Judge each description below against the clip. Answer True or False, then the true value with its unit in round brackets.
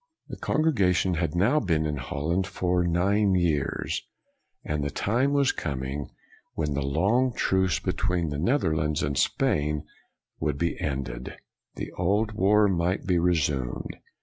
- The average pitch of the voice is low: True (85 Hz)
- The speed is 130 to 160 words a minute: True (150 wpm)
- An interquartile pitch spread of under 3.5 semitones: False (4.7 semitones)